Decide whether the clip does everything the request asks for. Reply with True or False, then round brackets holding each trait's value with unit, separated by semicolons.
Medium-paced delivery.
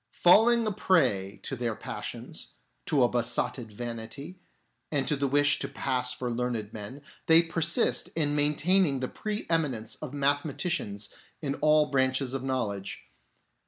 True (145 wpm)